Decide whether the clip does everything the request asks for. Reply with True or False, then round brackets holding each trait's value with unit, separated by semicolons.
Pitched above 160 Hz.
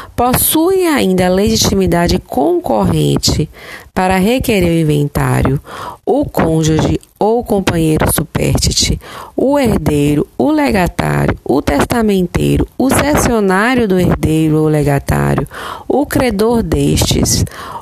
True (185 Hz)